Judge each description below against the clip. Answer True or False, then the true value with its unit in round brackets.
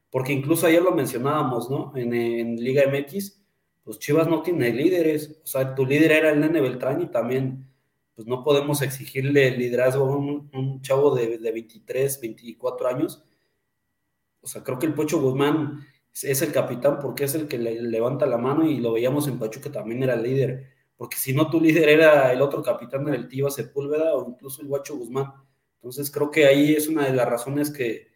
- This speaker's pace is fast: True (200 wpm)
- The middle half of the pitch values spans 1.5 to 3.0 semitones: True (2.7 semitones)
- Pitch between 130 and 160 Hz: True (140 Hz)